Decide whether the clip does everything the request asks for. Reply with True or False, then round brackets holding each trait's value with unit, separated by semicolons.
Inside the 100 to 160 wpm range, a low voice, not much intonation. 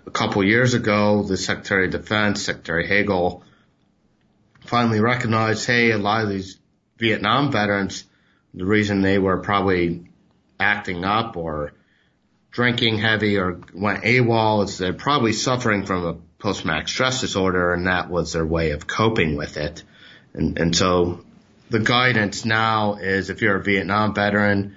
False (155 wpm; 100 Hz; 3.3 semitones)